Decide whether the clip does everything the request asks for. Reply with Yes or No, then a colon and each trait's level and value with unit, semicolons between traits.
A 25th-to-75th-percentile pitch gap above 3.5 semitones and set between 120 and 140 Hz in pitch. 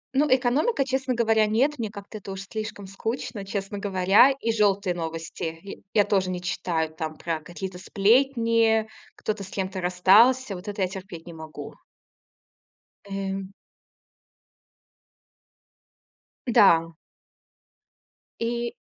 No: average, 3.9 semitones; high, 200 Hz